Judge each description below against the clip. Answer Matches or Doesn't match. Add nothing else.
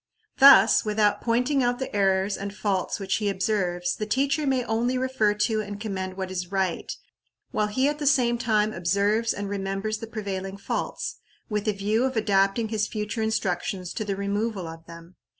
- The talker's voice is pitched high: Matches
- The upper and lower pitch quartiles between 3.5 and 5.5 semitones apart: Doesn't match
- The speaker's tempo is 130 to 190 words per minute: Matches